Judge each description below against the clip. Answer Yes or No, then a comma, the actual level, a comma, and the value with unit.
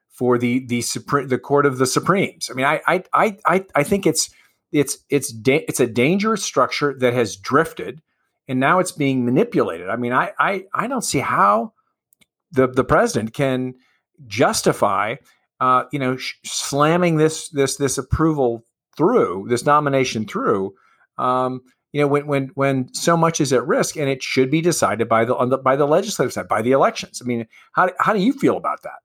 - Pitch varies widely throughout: No, average, 3.7 semitones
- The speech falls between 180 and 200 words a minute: Yes, average, 195 wpm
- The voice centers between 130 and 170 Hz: Yes, low, 135 Hz